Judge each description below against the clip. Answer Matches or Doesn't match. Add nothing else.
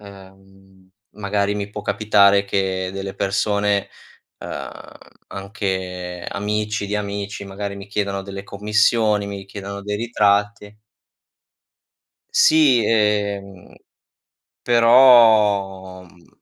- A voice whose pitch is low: Matches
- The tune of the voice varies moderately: Doesn't match